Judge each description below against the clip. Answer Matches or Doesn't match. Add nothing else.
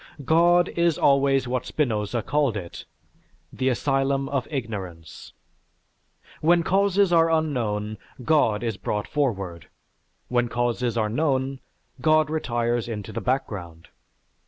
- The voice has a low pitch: Matches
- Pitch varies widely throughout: Matches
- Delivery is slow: Matches